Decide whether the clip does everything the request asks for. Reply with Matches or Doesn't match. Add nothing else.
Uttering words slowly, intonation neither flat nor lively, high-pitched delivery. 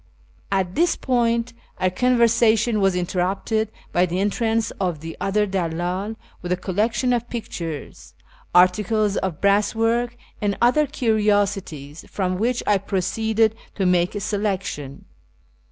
Matches